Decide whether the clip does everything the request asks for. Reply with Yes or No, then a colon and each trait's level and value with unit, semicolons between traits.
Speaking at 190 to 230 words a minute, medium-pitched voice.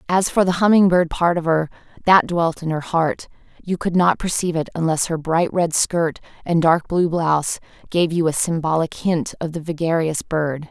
Yes: average, 200 wpm; medium, 165 Hz